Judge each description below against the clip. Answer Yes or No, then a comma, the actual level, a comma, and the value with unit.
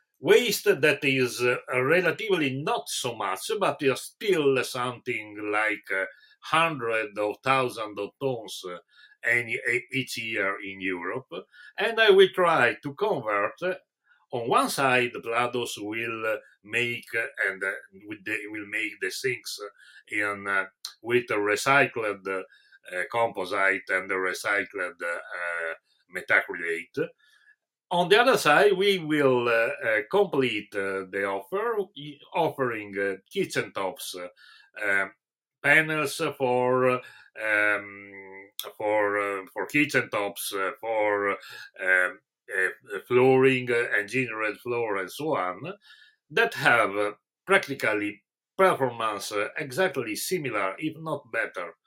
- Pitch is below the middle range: Yes, low, 125 Hz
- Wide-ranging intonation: Yes, wide, 7.1 semitones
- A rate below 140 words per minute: Yes, slow, 125 wpm